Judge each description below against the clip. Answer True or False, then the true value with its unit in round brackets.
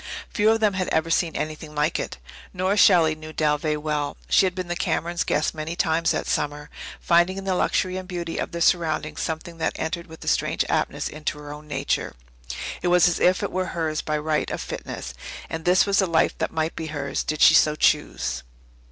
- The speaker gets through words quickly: True (215 wpm)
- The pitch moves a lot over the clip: False (2.7 semitones)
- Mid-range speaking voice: True (160 Hz)